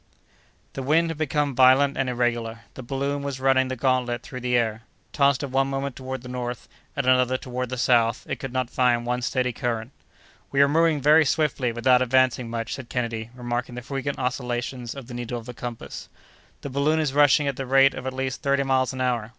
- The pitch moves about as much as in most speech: No, narrow, 2.0 semitones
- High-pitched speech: No, low, 130 Hz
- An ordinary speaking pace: No, fast, 215 wpm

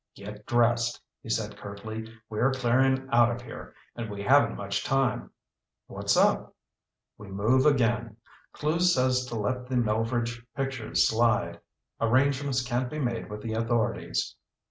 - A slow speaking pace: No, average, 145 wpm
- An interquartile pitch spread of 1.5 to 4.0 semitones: Yes, average, 2.8 semitones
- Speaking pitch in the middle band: No, low, 120 Hz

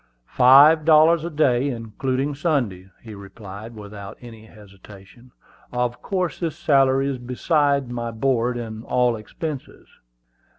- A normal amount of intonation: Yes, average, 4.4 semitones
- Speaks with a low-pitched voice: Yes, low, 125 Hz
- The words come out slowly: Yes, slow, 125 wpm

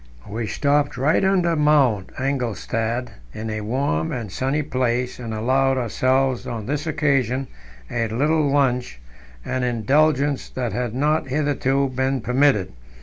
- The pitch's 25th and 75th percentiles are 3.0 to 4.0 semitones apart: Yes, average, 3.4 semitones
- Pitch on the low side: Yes, low, 130 Hz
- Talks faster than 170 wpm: No, slow, 135 wpm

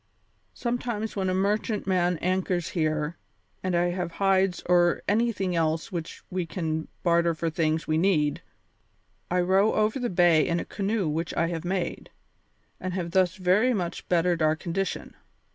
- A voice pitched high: No, medium, 180 Hz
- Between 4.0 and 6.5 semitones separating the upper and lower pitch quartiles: No, narrow, 2.6 semitones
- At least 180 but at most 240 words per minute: No, average, 160 wpm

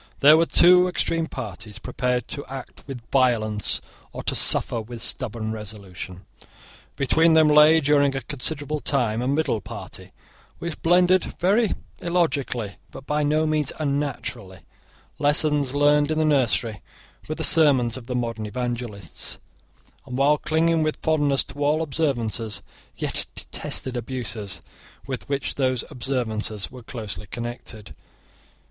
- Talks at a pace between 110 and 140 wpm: Yes, slow, 135 wpm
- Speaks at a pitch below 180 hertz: Yes, low, 135 Hz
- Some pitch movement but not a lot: Yes, average, 4.7 semitones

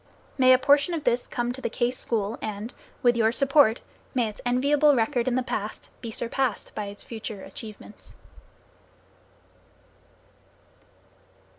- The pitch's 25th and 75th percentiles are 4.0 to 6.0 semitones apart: No, average, 3.0 semitones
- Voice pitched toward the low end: No, high, 240 Hz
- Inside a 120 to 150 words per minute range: Yes, average, 140 wpm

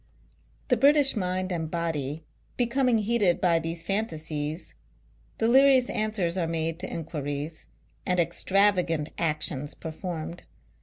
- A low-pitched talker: No, medium, 175 Hz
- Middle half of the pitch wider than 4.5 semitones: Yes, average, 5.0 semitones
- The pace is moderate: No, slow, 110 wpm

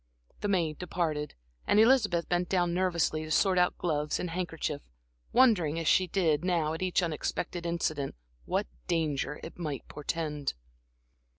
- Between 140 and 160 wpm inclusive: Yes, average, 150 wpm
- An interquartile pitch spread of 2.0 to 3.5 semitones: Yes, average, 2.8 semitones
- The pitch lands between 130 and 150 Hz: No, medium, 170 Hz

